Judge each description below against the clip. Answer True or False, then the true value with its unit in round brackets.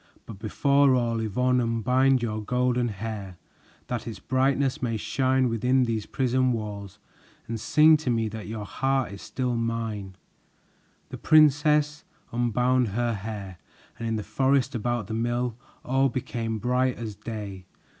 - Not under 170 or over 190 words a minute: False (145 wpm)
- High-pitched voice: False (120 Hz)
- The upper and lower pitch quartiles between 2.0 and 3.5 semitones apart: True (2.9 semitones)